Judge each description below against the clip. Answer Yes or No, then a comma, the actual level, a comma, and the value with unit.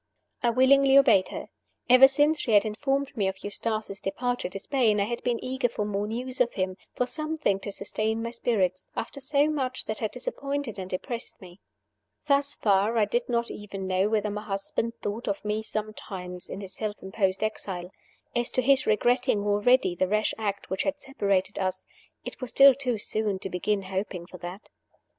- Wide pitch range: No, average, 4.4 semitones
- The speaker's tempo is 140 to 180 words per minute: No, average, 190 wpm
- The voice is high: Yes, high, 215 Hz